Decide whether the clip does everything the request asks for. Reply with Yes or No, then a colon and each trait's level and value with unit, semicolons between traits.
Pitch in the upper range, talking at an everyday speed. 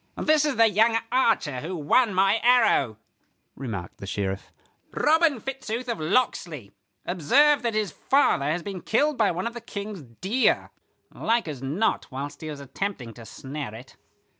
Yes: high, 195 Hz; average, 165 wpm